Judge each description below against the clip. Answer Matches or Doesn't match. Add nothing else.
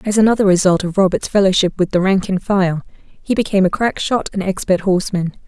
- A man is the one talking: Doesn't match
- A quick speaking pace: Matches